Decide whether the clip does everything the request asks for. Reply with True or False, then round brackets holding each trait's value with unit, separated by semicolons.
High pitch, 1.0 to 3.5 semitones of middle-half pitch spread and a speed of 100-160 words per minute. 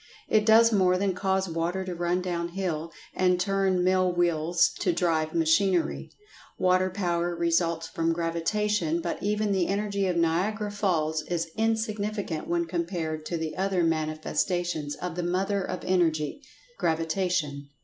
False (175 Hz; 2.7 semitones; 140 wpm)